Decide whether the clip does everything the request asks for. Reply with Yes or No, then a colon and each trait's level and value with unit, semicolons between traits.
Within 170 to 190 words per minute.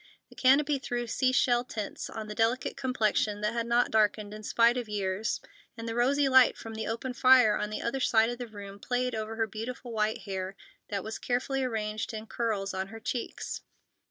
No: fast, 205 wpm